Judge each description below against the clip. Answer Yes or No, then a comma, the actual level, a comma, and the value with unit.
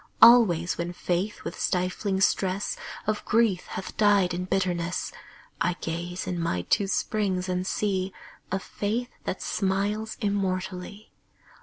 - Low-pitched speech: No, high, 190 Hz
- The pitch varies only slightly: Yes, narrow, 2.3 semitones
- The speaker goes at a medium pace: No, slow, 130 wpm